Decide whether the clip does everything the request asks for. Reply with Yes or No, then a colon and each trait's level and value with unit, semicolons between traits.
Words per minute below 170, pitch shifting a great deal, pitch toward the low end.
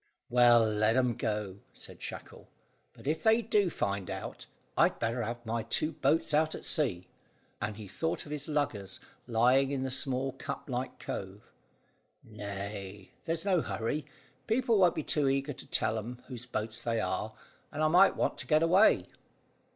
No: average, 175 wpm; wide, 5.8 semitones; low, 125 Hz